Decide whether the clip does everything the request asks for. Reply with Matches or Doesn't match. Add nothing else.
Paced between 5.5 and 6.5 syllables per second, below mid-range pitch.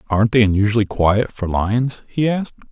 Matches